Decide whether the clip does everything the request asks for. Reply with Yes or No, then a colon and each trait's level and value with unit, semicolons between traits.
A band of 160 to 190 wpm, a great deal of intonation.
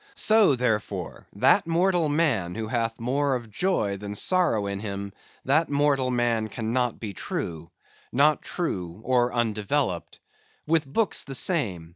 No: slow, 135 wpm; wide, 6.1 semitones